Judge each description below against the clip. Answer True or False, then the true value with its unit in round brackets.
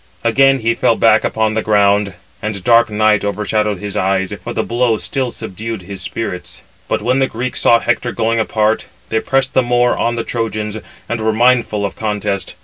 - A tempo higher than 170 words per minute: True (190 wpm)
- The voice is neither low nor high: False (110 Hz)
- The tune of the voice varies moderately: False (2.3 semitones)